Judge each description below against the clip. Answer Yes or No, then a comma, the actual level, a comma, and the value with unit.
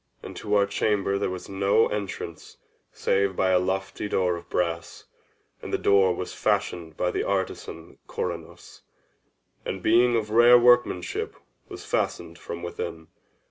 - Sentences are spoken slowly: No, average, 145 wpm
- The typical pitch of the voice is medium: No, very low, 95 Hz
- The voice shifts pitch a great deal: No, average, 2.7 semitones